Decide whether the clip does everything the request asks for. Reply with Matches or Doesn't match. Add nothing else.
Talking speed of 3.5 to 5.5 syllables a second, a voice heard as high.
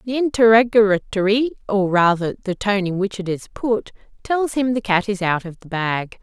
Matches